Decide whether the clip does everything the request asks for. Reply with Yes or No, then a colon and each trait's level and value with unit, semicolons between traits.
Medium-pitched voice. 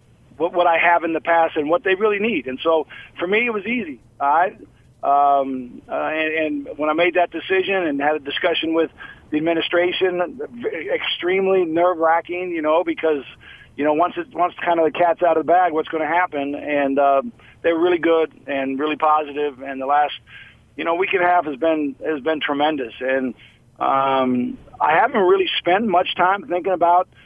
Yes: medium, 165 Hz